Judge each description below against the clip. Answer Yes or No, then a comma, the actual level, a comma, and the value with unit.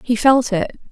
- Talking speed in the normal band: Yes, average, 195 wpm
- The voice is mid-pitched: No, high, 235 Hz